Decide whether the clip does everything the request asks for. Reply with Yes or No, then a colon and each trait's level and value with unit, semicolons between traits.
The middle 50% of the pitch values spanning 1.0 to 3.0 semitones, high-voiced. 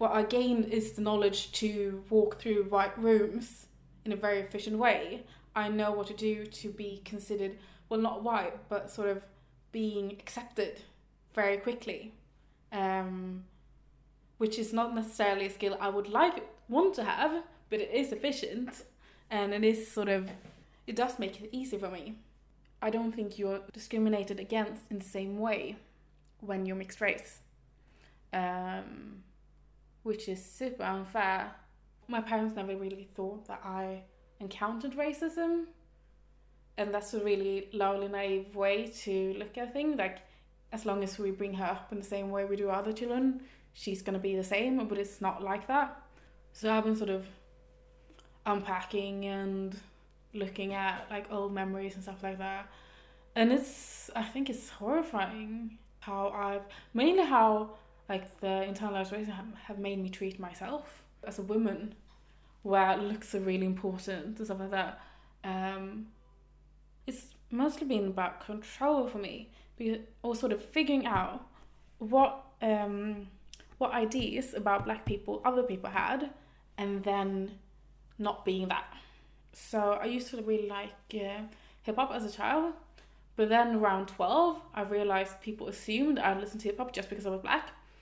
Yes: narrow, 2.6 semitones; high, 205 Hz